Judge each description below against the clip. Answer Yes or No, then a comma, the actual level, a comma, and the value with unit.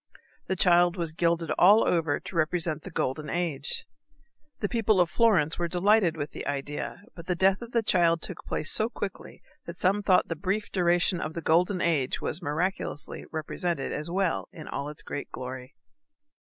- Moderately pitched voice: Yes, medium, 170 Hz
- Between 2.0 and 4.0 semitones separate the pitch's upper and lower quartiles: Yes, average, 3.4 semitones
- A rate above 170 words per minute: Yes, average, 180 wpm